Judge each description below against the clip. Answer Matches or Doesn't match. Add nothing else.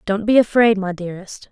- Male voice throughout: Doesn't match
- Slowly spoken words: Doesn't match